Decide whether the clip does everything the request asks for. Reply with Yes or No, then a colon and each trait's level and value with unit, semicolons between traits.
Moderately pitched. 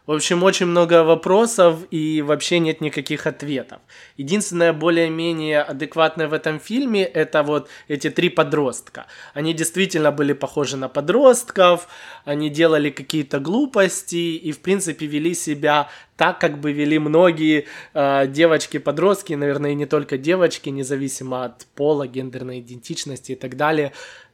Yes: medium, 155 Hz